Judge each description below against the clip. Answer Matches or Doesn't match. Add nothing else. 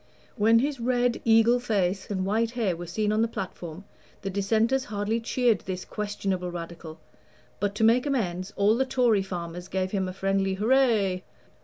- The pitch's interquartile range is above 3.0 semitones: Matches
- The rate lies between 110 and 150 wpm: Doesn't match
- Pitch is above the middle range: Matches